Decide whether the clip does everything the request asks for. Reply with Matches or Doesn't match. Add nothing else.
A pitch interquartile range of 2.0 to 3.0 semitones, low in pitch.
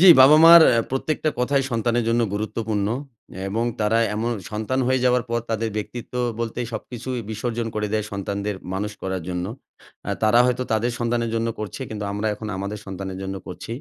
Matches